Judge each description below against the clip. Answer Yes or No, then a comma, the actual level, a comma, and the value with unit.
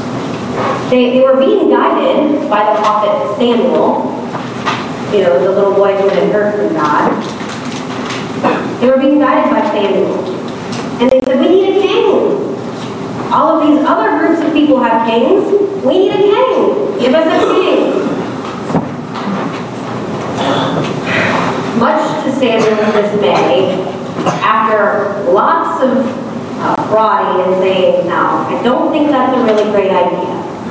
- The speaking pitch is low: No, very high, 250 Hz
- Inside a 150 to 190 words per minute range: No, slow, 135 wpm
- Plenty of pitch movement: Yes, wide, 6.6 semitones